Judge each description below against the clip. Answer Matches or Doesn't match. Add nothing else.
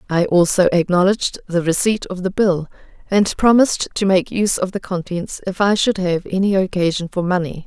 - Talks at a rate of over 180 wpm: Matches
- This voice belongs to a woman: Matches